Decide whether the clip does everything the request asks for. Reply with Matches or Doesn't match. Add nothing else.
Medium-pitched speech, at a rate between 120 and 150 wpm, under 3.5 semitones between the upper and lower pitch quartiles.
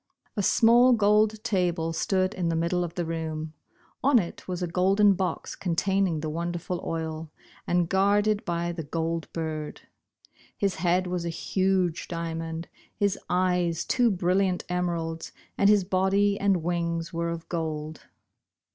Matches